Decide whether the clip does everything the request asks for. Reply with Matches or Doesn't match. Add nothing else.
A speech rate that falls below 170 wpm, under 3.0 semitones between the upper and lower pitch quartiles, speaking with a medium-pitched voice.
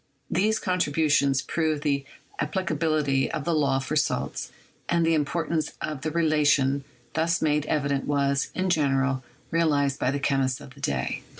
Matches